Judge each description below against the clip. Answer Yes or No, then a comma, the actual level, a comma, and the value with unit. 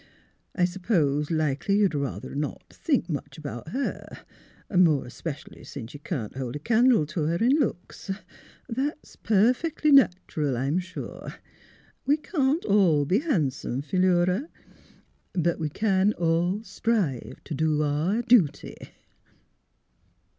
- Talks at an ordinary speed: No, slow, 125 wpm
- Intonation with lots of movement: Yes, wide, 6.9 semitones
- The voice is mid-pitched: Yes, medium, 175 Hz